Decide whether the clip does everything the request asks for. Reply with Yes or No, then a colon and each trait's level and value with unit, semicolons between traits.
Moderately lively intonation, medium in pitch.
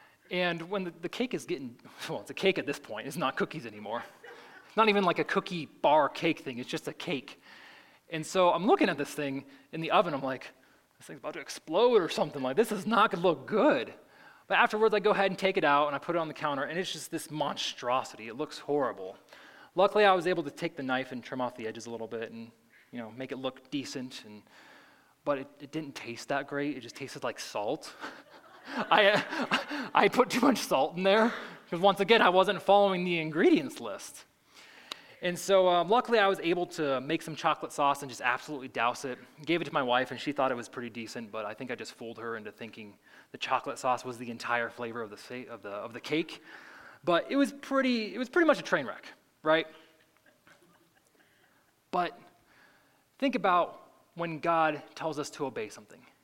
No: wide, 6.8 semitones; medium, 155 Hz